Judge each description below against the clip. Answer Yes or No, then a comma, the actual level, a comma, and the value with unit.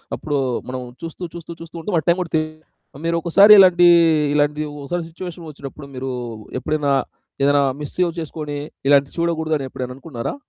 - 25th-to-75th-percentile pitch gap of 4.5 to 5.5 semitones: No, average, 2.9 semitones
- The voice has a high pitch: No, medium, 155 Hz